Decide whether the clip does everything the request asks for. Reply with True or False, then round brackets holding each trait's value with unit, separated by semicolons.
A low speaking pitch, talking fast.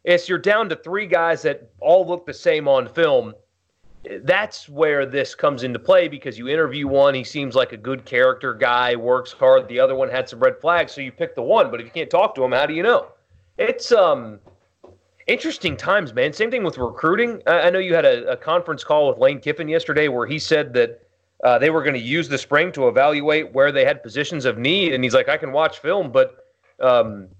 False (175 Hz; 230 wpm)